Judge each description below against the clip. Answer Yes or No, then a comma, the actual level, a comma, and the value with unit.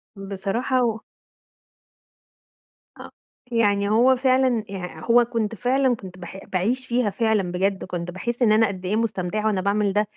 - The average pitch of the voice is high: Yes, high, 215 Hz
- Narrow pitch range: No, average, 3.8 semitones